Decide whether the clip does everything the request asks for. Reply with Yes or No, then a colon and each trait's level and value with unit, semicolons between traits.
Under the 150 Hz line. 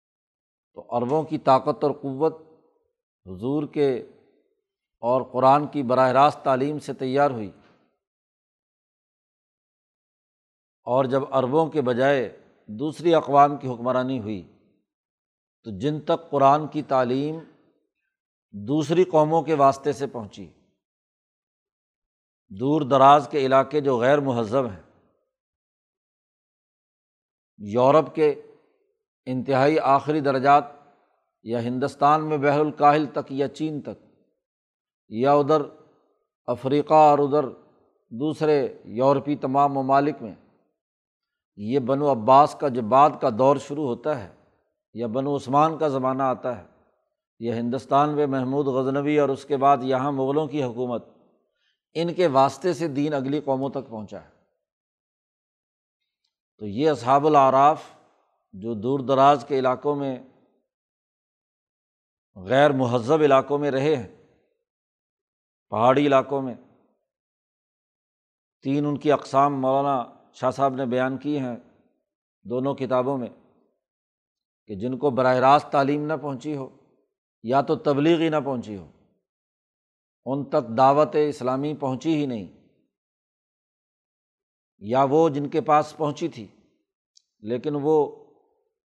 Yes: medium, 140 Hz